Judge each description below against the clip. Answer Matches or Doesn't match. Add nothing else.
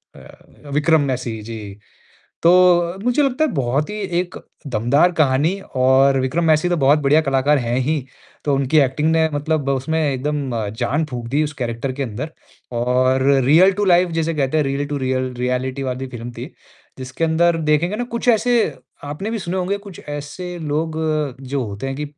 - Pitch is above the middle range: Doesn't match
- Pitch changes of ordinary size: Matches